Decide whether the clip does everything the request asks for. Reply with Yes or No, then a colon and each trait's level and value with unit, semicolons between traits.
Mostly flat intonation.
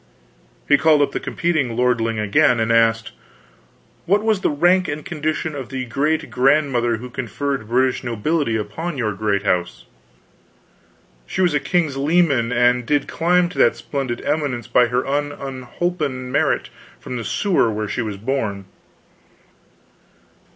No: average, 4.7 semitones